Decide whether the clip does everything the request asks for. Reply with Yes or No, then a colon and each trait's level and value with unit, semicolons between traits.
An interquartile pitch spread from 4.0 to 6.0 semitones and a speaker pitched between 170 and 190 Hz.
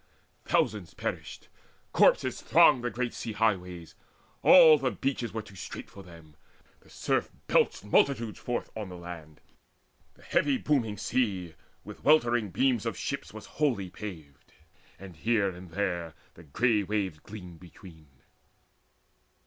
No: average, 5.3 semitones; low, 100 Hz